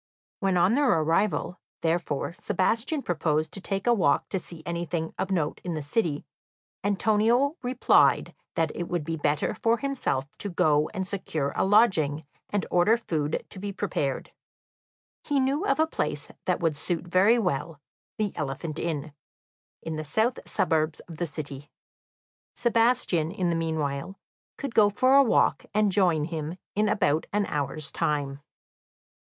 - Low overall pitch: No, medium, 175 Hz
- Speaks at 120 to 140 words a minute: No, average, 160 wpm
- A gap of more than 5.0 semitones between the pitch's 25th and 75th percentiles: Yes, wide, 5.4 semitones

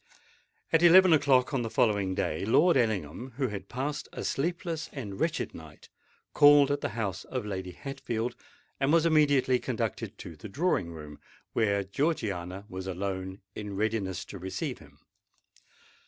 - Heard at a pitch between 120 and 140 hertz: No, low, 110 Hz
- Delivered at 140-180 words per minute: Yes, average, 155 wpm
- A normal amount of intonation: No, wide, 7.1 semitones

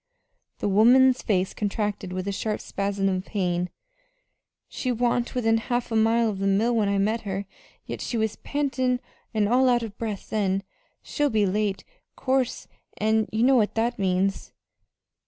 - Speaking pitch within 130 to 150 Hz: No, high, 220 Hz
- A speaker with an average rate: Yes, average, 170 wpm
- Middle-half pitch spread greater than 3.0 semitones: Yes, average, 3.4 semitones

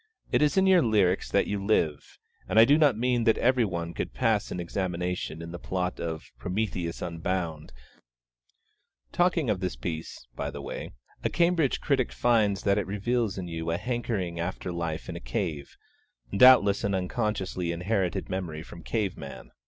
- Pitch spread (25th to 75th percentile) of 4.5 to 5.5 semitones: Yes, average, 5.1 semitones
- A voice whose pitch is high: No, very low, 95 Hz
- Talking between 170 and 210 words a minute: Yes, average, 175 wpm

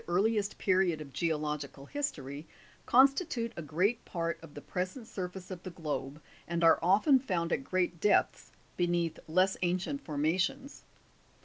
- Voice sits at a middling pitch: Yes, medium, 180 Hz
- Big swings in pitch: No, average, 4.0 semitones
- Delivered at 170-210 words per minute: No, average, 140 wpm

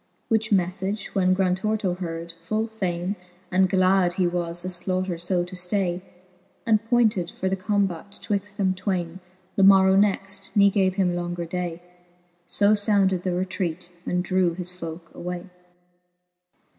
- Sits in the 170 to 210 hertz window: Yes, medium, 185 Hz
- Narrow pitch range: Yes, narrow, 2.0 semitones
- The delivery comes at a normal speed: Yes, average, 145 wpm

